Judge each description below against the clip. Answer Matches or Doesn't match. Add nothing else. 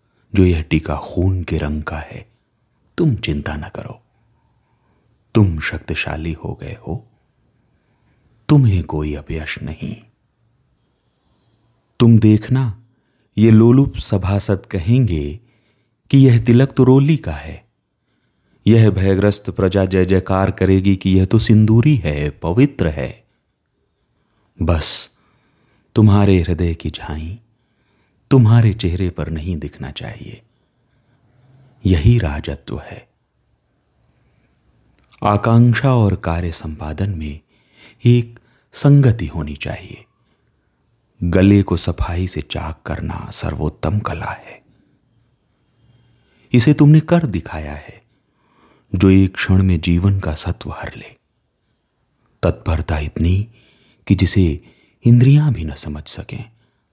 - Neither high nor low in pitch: Doesn't match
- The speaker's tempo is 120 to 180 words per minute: Doesn't match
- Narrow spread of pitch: Doesn't match